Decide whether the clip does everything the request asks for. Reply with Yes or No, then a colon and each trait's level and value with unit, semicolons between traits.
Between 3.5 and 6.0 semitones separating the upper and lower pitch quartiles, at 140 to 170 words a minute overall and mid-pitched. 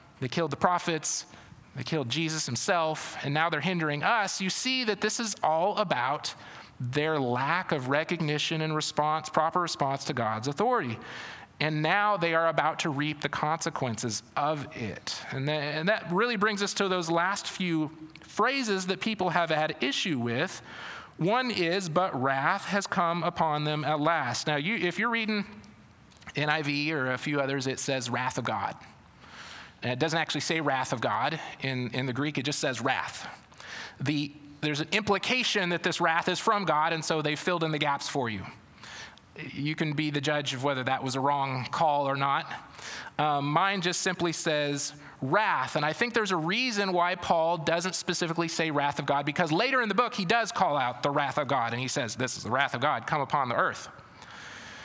No: average, 3.9 semitones; average, 195 wpm; medium, 155 Hz